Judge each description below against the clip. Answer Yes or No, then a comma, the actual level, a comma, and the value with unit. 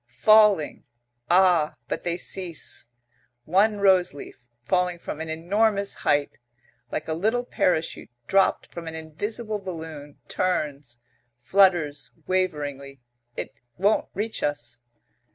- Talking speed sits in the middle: No, slow, 115 wpm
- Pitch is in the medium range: Yes, medium, 175 Hz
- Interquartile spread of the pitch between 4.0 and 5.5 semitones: Yes, average, 4.6 semitones